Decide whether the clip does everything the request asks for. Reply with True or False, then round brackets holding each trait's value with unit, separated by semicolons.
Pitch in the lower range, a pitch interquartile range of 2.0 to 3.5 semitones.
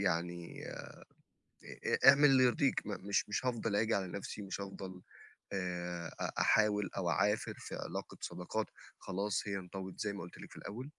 True (100 Hz; 2.9 semitones)